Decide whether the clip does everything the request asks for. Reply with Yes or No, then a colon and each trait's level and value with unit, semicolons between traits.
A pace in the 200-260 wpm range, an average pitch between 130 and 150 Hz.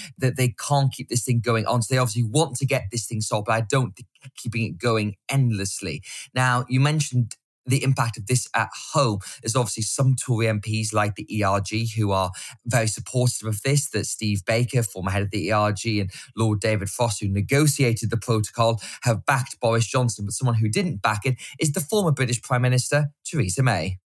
No: fast, 205 wpm; low, 120 Hz